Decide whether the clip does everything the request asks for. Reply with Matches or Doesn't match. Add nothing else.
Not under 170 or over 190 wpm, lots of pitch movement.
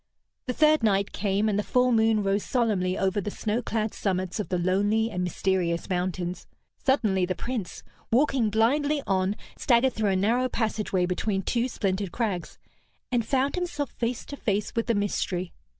Doesn't match